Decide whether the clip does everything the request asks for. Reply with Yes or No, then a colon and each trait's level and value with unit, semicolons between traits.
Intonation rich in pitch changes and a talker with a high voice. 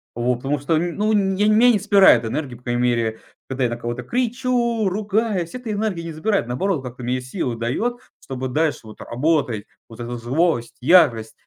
No: wide, 8.9 semitones; medium, 150 Hz